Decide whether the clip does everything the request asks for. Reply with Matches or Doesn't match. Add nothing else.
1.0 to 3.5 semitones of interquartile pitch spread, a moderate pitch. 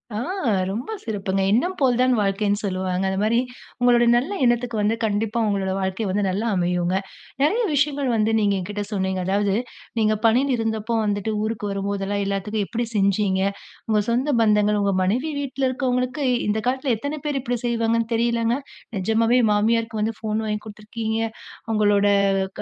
Doesn't match